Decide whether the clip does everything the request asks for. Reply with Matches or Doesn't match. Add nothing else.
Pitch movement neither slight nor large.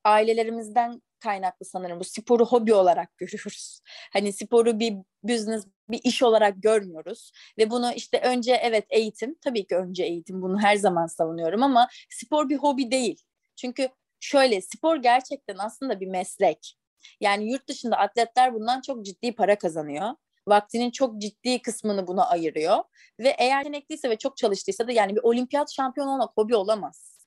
Matches